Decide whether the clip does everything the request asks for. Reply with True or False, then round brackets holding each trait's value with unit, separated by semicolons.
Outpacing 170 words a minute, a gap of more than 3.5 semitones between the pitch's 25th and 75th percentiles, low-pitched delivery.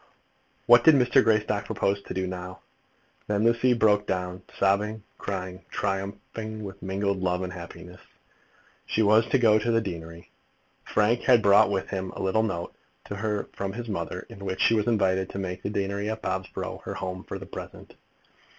False (180 wpm; 2.7 semitones; 100 Hz)